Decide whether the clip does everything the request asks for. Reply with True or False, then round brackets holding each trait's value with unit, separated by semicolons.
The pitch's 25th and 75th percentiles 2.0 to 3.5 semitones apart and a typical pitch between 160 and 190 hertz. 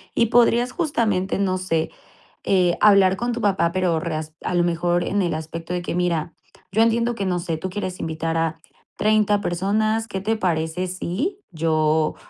False (4.1 semitones; 185 Hz)